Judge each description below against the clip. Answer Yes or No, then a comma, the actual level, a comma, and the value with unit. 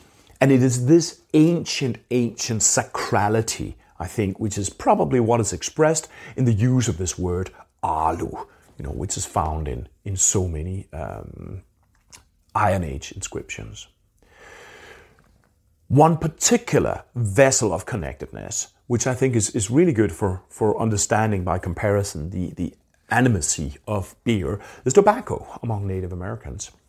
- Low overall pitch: Yes, low, 105 Hz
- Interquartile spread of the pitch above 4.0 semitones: Yes, average, 5.2 semitones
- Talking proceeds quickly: No, average, 140 wpm